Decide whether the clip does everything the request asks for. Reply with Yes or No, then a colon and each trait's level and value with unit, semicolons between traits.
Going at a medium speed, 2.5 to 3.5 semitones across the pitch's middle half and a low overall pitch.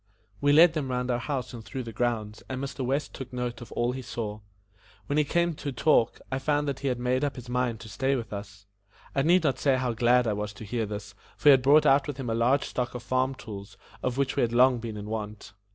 No: fast, 265 wpm; average, 3.2 semitones; low, 125 Hz